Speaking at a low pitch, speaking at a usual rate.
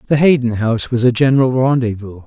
Yes: low, 120 Hz; average, 185 wpm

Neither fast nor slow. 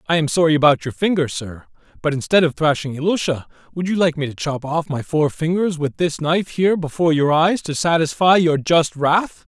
No: fast, 215 wpm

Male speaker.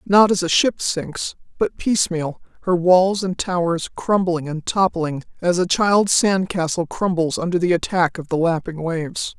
No: female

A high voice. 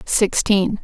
Yes: high, 205 Hz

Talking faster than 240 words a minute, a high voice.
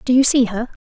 Yes: fast, 290 wpm; high, 245 Hz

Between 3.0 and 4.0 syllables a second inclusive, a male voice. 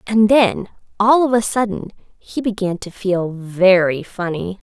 No: 3.9 syllables/s; female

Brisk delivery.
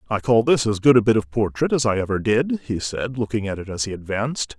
Yes: fast, 275 wpm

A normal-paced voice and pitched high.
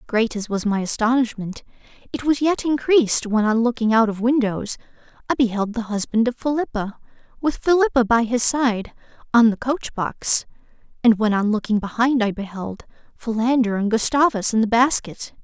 Yes: average, 165 wpm; high, 235 Hz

